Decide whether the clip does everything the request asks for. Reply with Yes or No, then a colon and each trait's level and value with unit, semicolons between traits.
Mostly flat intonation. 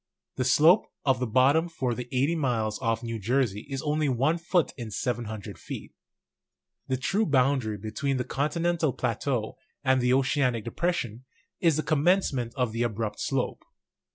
No: average, 4.1 semitones